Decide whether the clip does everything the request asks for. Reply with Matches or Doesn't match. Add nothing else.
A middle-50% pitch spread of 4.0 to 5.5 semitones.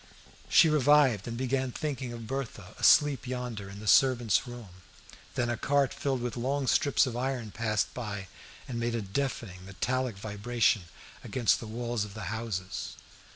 Doesn't match